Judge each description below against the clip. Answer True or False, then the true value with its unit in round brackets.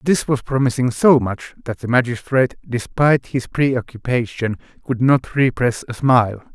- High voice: False (125 Hz)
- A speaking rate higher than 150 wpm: False (145 wpm)